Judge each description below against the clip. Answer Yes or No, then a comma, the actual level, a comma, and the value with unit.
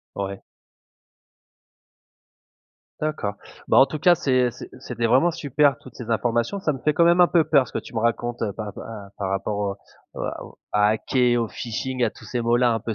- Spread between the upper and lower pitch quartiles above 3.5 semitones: Yes, average, 4.1 semitones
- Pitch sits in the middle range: No, low, 120 Hz